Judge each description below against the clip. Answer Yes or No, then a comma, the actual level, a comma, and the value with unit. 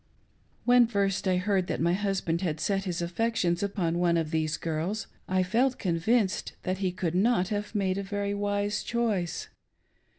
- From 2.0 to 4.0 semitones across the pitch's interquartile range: Yes, average, 2.9 semitones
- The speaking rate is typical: Yes, average, 170 wpm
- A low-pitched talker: No, high, 190 Hz